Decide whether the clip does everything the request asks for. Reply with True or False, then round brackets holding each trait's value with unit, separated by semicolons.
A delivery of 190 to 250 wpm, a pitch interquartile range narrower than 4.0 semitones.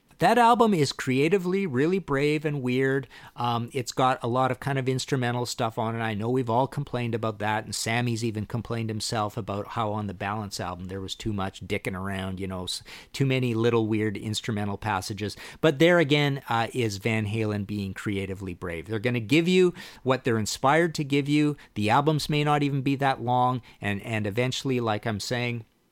False (200 wpm; 4.6 semitones)